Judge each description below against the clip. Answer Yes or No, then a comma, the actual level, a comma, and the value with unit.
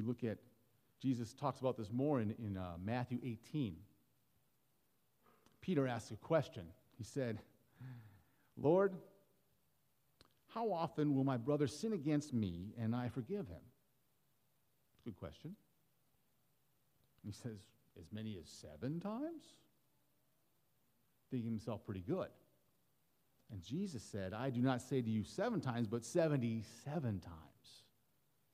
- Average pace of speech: No, slow, 125 wpm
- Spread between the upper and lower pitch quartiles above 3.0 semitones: Yes, average, 4.9 semitones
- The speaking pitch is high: No, low, 125 Hz